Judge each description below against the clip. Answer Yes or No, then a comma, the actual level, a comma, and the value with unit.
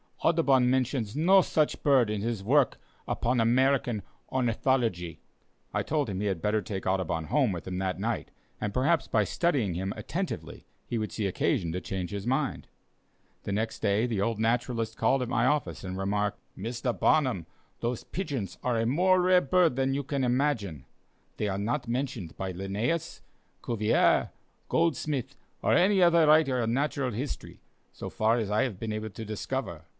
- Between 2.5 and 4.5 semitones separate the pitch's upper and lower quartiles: No, average, 5.1 semitones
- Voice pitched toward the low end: Yes, low, 120 Hz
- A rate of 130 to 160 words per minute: No, average, 170 wpm